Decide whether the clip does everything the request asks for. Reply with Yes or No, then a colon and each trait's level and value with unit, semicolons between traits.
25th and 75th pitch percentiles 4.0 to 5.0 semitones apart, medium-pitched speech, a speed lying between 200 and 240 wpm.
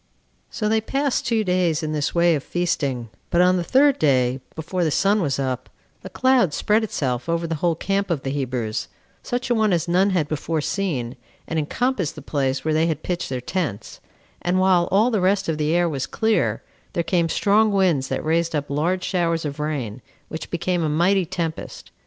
Yes: average, 4.3 semitones; medium, 170 Hz; fast, 205 wpm